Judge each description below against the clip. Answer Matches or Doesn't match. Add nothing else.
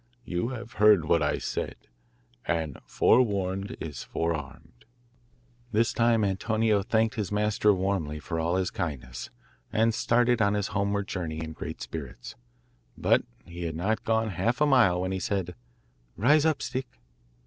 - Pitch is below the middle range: Matches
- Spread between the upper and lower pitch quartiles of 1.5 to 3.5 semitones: Doesn't match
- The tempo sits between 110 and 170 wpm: Matches